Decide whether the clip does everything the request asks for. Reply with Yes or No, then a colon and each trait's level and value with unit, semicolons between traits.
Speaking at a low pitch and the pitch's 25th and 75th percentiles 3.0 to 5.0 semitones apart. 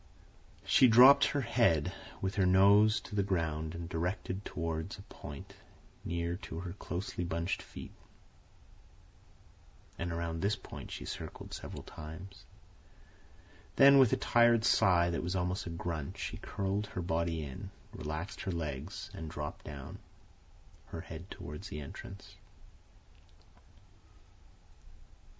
Yes: very low, 85 Hz; average, 3.4 semitones